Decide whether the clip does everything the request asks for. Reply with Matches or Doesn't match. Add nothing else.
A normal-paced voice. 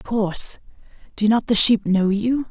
Matches